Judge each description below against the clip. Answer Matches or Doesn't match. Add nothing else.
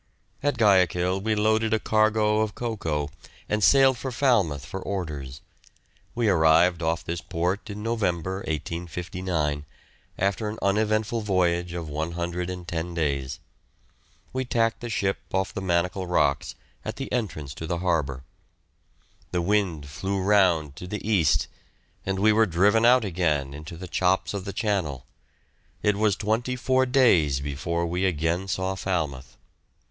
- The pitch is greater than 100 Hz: Doesn't match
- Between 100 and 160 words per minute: Matches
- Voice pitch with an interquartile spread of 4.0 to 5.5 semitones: Matches